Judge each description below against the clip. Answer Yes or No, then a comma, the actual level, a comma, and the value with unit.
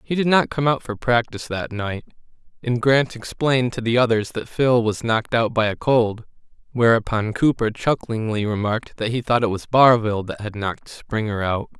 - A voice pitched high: No, low, 115 Hz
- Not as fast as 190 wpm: No, average, 195 wpm